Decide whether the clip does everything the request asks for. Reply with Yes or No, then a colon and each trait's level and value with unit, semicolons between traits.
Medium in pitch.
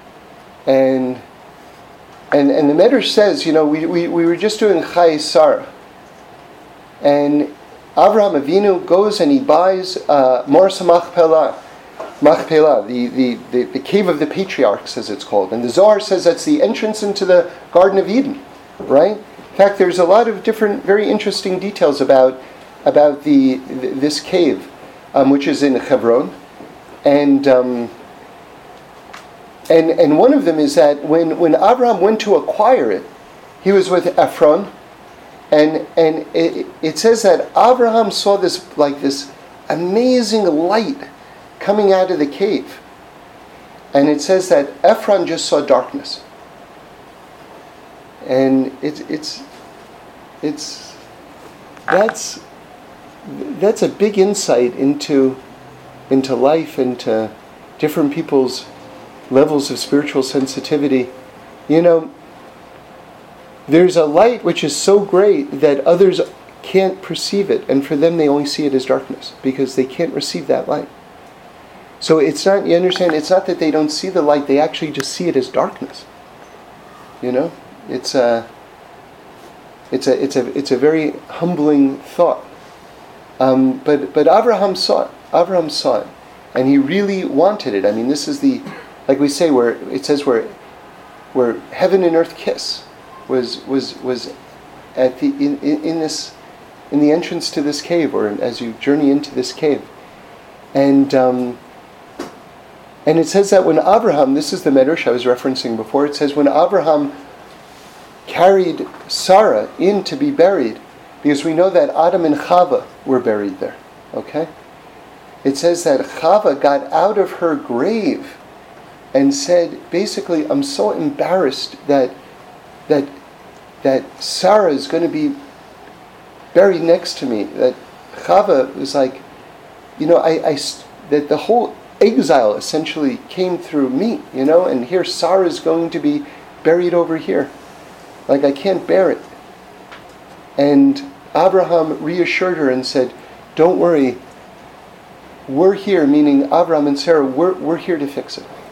Yes: medium, 160 Hz